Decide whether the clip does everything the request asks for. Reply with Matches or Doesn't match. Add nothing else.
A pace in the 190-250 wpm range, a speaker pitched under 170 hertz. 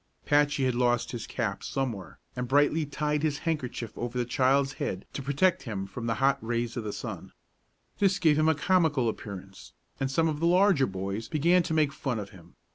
Matches